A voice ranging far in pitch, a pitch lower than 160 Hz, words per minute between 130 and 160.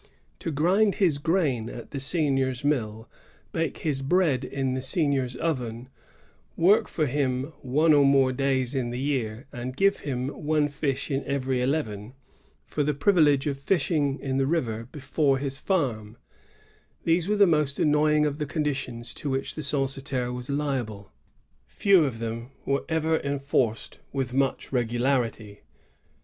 No: average, 3.1 semitones; medium, 140 Hz; average, 155 wpm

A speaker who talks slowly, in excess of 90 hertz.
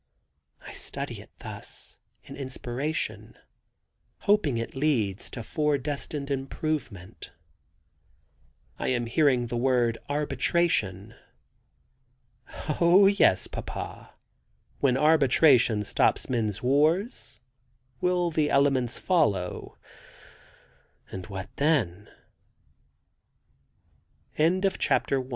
Yes: slow, 85 wpm; low, 135 Hz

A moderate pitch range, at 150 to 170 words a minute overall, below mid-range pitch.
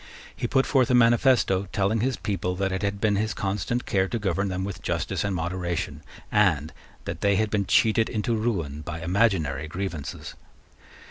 No: average, 3.4 semitones; average, 180 wpm; low, 100 Hz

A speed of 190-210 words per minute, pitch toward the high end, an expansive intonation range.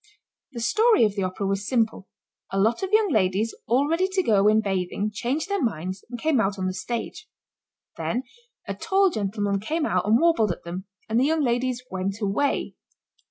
Yes: average, 195 wpm; high, 225 Hz; wide, 6.4 semitones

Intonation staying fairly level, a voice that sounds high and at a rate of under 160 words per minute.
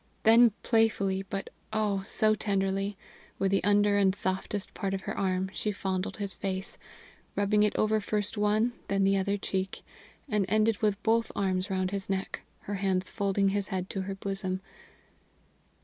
No: narrow, 1.5 semitones; high, 200 Hz; average, 165 wpm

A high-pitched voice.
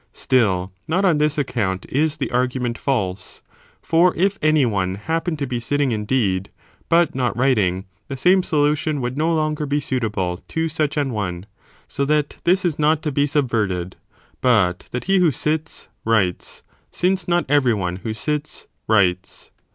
No: low, 135 Hz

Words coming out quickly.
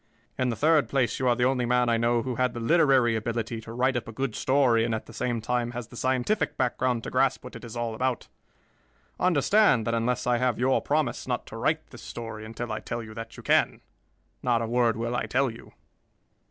Yes: fast, 235 wpm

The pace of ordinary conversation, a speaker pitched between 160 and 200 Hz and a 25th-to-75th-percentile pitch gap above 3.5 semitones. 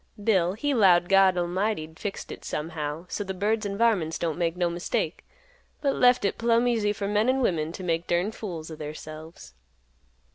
Yes: average, 190 wpm; medium, 185 Hz; average, 4.4 semitones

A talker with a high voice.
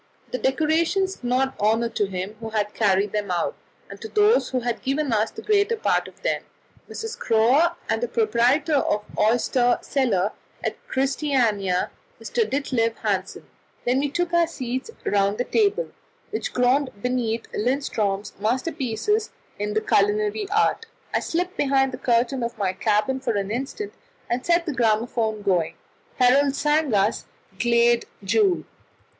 Yes: high, 245 Hz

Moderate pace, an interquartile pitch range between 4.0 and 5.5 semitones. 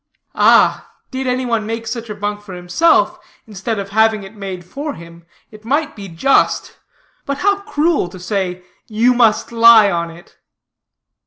Yes: average, 165 wpm; average, 4.6 semitones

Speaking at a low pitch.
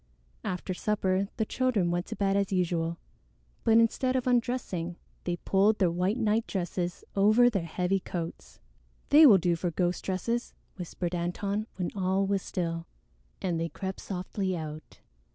No: high, 190 Hz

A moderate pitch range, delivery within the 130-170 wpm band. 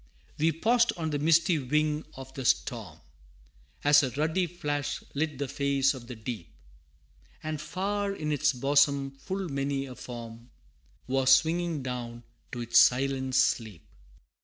Yes: average, 3.3 semitones; average, 145 wpm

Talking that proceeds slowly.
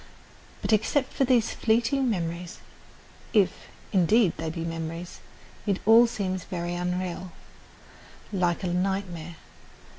Yes: slow, 115 wpm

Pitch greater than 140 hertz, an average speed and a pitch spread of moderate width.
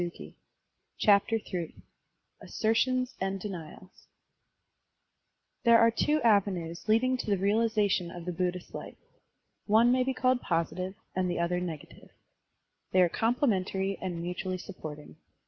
No: high, 190 Hz; slow, 130 wpm; average, 4.2 semitones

